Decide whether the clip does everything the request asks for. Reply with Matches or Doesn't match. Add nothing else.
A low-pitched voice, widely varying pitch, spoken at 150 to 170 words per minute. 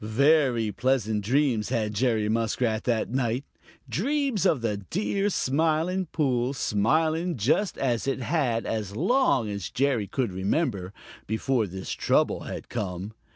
Doesn't match